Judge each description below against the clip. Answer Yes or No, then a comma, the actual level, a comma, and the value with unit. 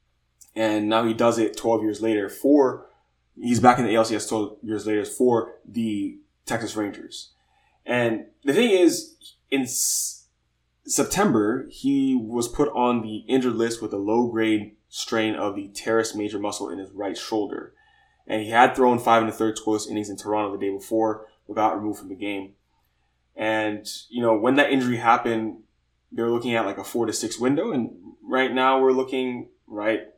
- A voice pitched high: No, low, 110 Hz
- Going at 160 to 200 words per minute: Yes, average, 180 wpm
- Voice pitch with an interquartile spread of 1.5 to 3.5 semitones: Yes, narrow, 2.6 semitones